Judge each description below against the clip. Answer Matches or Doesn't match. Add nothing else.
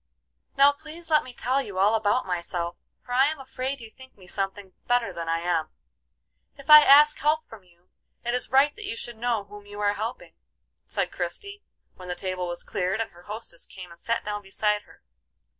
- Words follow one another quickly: Matches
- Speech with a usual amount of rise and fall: Doesn't match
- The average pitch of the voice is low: Doesn't match